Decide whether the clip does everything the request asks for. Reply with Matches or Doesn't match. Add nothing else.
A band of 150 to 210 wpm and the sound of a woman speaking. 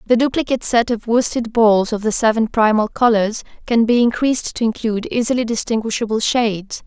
Matches